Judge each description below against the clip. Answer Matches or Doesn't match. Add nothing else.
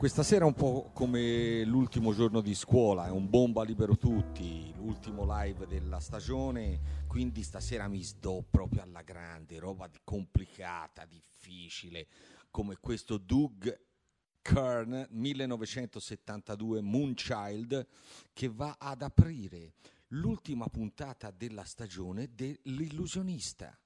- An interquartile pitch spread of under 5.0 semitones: Doesn't match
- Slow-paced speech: Matches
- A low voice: Matches